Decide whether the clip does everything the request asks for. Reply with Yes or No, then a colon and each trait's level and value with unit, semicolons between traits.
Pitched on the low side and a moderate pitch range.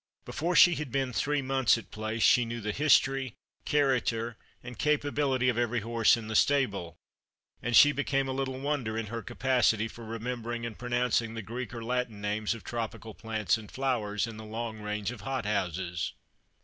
Yes: low, 120 Hz; average, 3.3 semitones